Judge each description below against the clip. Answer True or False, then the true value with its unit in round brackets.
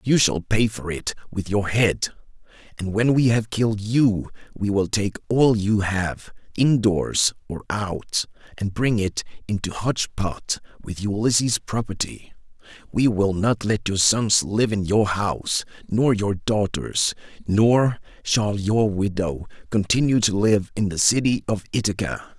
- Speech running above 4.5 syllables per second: False (4.0 syllables/s)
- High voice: False (105 Hz)